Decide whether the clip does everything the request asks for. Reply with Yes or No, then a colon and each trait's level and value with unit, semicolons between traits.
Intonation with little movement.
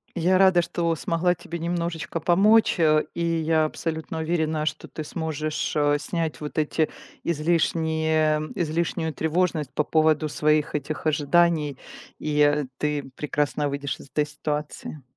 Yes: narrow, 1.9 semitones